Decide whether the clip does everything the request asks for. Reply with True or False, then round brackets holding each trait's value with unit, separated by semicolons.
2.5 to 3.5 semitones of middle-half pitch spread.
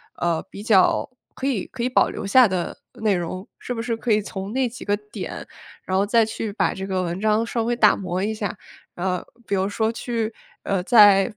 True (3.1 semitones)